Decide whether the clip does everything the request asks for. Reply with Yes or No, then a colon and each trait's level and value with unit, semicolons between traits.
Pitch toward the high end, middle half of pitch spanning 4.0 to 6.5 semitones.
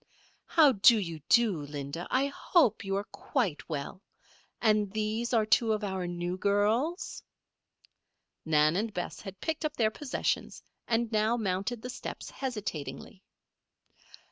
Yes: high, 215 Hz; average, 4.4 semitones